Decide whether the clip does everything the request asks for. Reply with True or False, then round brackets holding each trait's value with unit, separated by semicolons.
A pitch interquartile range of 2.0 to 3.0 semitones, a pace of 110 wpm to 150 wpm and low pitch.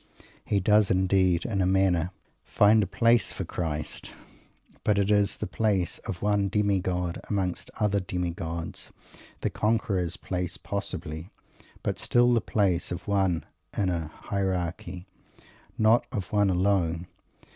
True (2.6 semitones; 140 wpm; 95 Hz)